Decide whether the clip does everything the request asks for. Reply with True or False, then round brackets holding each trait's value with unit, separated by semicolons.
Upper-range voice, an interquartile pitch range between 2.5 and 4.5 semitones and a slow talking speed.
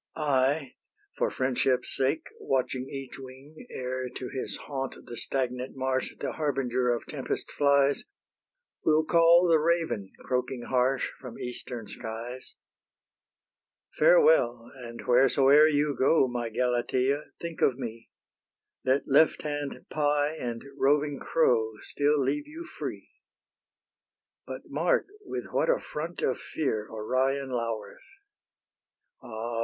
False (135 Hz; 3.2 semitones; 120 wpm)